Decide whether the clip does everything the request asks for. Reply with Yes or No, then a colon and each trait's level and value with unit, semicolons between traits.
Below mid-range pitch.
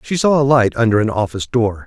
Yes: low, 120 Hz